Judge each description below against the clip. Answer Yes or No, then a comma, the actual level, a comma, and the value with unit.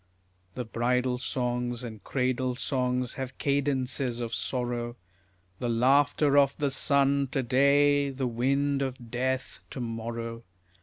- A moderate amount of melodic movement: No, narrow, 2.3 semitones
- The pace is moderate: No, slow, 125 wpm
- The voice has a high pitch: No, low, 125 Hz